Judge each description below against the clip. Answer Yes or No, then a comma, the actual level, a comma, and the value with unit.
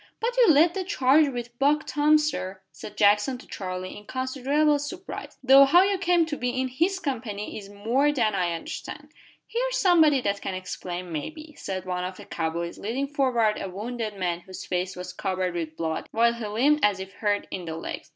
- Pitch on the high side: Yes, high, 235 Hz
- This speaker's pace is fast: Yes, fast, 210 wpm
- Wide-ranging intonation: Yes, wide, 7.8 semitones